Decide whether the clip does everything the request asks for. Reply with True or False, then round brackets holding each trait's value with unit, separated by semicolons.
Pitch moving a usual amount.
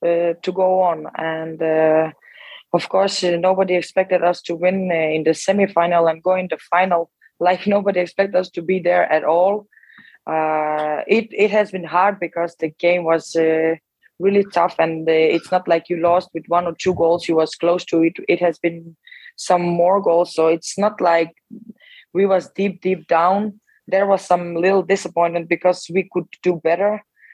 False (2.3 semitones)